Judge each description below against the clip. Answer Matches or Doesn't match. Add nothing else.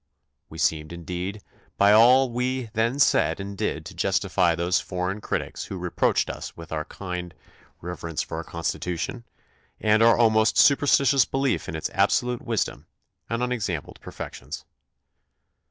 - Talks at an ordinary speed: Matches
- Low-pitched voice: Matches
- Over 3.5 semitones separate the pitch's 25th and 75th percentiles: Matches